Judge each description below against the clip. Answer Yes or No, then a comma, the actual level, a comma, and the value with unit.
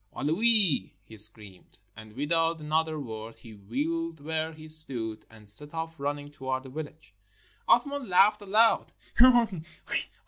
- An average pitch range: No, wide, 6.1 semitones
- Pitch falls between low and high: Yes, medium, 150 Hz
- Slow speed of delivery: Yes, slow, 130 wpm